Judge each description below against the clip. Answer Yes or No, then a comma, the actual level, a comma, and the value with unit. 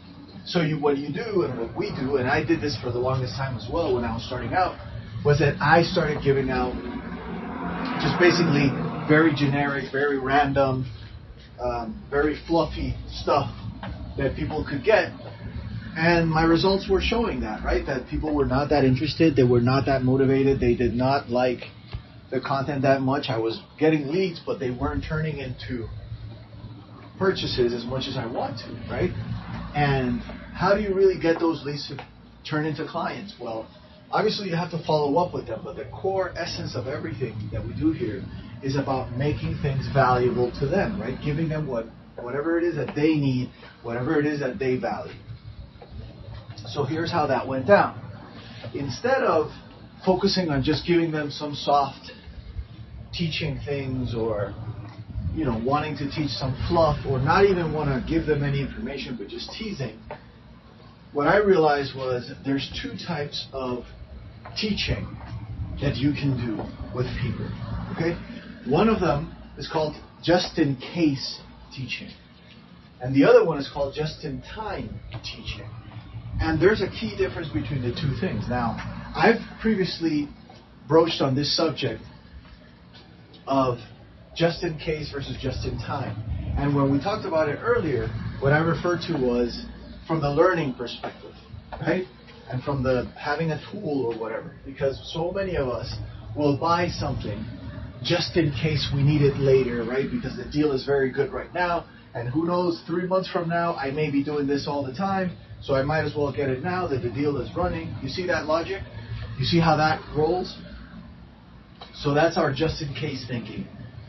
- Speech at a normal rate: Yes, average, 175 wpm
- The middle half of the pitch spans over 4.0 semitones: Yes, average, 4.6 semitones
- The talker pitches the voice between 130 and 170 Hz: Yes, medium, 140 Hz